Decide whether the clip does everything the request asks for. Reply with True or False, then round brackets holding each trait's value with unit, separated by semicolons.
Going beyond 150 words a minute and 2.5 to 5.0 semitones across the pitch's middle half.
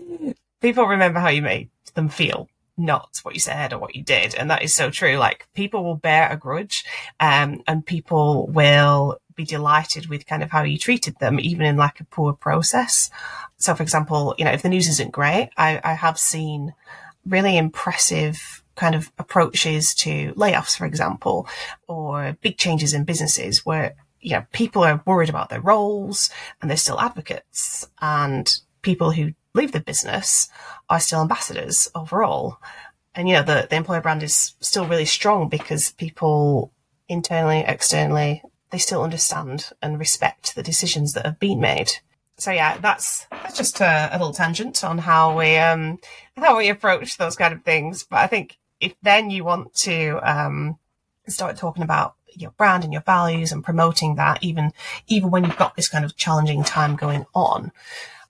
True (180 wpm; 3.0 semitones)